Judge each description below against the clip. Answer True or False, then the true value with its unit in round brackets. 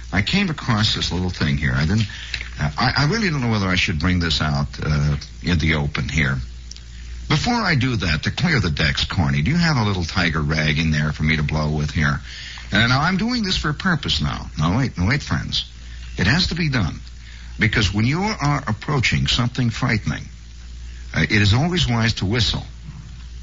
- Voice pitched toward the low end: True (85 Hz)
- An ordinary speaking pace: False (210 wpm)